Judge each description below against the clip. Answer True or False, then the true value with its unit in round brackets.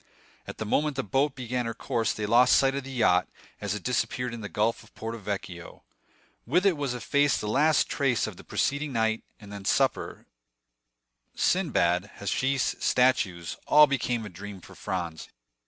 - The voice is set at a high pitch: False (115 Hz)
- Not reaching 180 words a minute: True (170 wpm)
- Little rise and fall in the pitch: False (4.8 semitones)